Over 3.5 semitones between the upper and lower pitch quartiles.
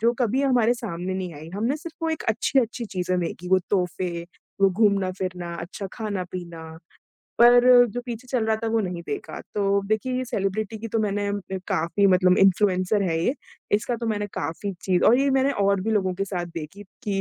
Yes: average, 4.0 semitones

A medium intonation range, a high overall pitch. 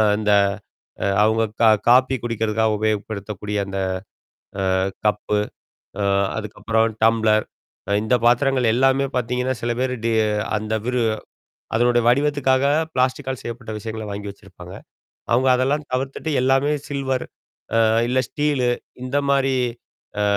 No: average, 3.3 semitones; low, 120 Hz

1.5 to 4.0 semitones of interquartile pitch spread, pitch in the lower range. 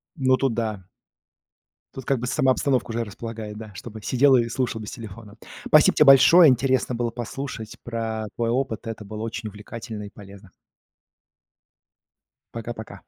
Yes: average, 2.8 semitones; low, 115 Hz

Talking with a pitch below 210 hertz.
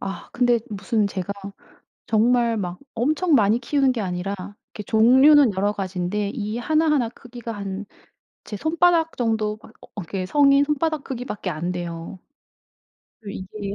No: high, 220 Hz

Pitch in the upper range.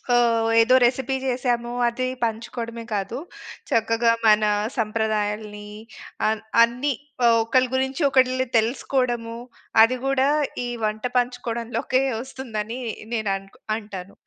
Yes: high, 235 Hz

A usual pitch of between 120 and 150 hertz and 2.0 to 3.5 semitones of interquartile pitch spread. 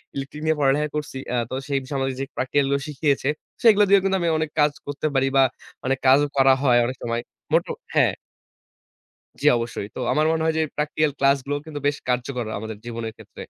Yes: medium, 140 Hz; narrow, 2.6 semitones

